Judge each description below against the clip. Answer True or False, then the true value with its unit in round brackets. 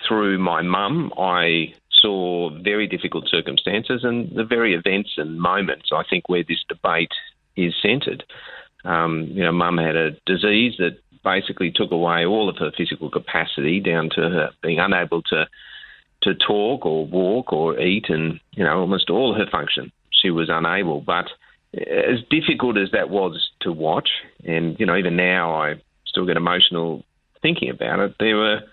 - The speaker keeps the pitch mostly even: False (4.1 semitones)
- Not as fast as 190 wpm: True (170 wpm)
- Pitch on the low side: True (90 Hz)